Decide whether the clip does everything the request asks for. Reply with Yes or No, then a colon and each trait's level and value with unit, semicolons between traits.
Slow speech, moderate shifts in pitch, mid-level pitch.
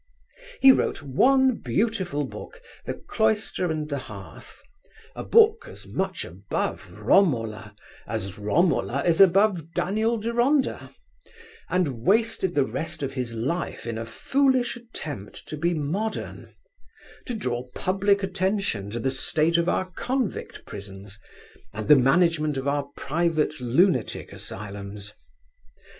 No: slow, 125 wpm; wide, 8.2 semitones; medium, 165 Hz